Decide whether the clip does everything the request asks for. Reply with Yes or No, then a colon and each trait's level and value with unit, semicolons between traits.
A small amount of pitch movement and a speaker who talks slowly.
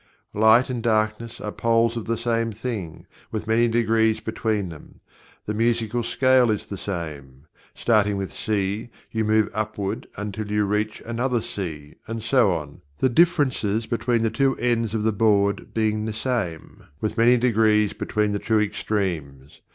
No: narrow, 2.1 semitones; average, 160 wpm